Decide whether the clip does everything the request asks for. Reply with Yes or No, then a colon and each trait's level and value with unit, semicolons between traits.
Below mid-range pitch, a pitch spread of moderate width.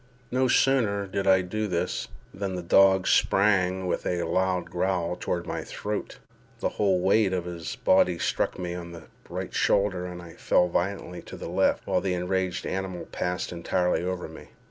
No: very low, 90 Hz; narrow, 1.6 semitones